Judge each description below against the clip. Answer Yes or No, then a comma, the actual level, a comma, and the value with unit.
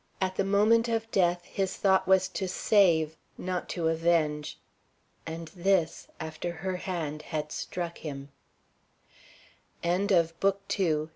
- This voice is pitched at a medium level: Yes, medium, 175 Hz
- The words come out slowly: Yes, slow, 130 wpm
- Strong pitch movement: No, average, 3.1 semitones